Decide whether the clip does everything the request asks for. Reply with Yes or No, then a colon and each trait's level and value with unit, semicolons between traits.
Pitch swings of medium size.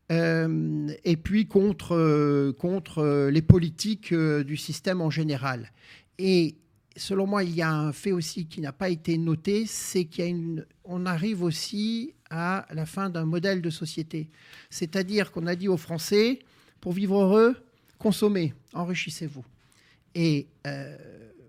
Yes: average, 3.7 semitones